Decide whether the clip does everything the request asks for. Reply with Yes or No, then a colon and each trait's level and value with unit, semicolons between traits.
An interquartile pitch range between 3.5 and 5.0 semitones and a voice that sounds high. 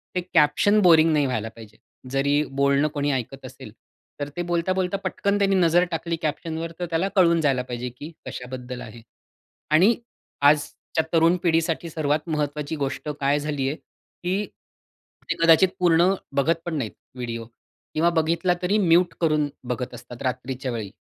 No: average, 4.1 semitones; medium, 155 Hz